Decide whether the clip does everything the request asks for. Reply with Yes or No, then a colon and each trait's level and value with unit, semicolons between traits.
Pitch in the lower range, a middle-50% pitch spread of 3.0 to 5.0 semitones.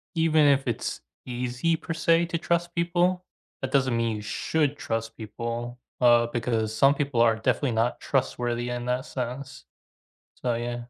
Yes: low, 125 Hz; average, 4.0 semitones